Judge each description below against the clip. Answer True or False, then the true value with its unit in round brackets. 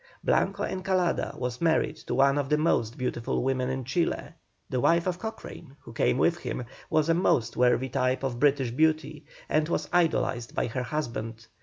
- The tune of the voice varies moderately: True (4.7 semitones)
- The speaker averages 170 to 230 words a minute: True (180 wpm)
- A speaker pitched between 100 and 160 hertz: True (135 Hz)